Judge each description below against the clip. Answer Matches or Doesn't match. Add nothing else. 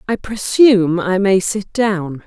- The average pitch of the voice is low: Doesn't match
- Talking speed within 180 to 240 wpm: Doesn't match